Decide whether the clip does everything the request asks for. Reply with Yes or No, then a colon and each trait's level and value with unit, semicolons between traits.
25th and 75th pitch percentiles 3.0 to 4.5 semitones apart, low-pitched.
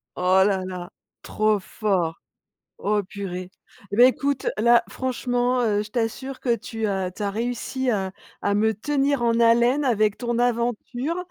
No: average, 3.4 semitones; high, 225 Hz